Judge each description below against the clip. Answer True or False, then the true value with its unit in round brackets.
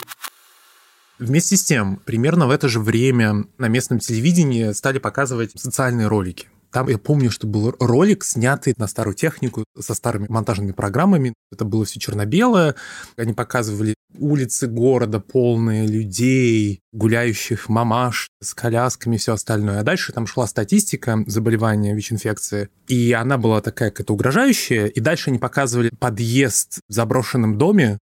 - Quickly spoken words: False (145 wpm)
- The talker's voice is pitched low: True (115 Hz)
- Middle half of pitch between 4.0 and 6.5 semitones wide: False (3.2 semitones)